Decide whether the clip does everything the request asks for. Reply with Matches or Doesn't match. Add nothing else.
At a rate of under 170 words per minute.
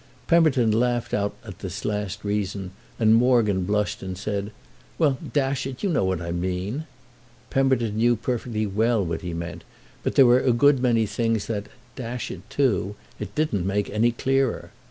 Matches